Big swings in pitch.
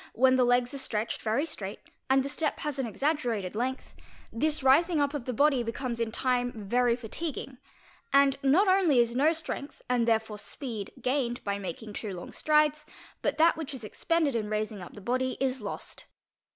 No: average, 4.2 semitones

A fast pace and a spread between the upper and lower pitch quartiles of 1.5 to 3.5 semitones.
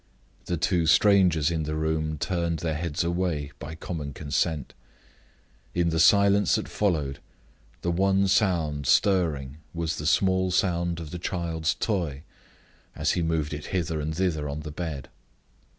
No: average, 150 wpm; average, 2.9 semitones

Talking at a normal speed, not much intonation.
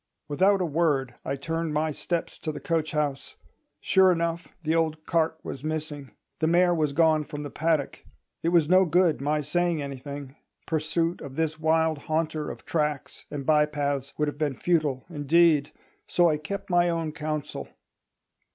Yes: average, 170 wpm; narrow, 2.2 semitones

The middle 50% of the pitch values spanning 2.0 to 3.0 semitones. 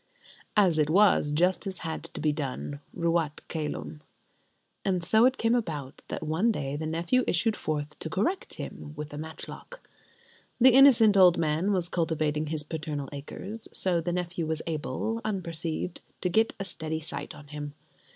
No: average, 4.3 semitones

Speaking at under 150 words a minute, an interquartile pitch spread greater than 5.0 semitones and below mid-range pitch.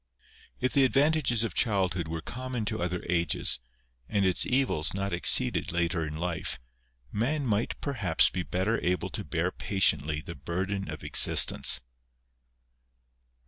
Yes: average, 140 wpm; wide, 5.4 semitones; very low, 95 Hz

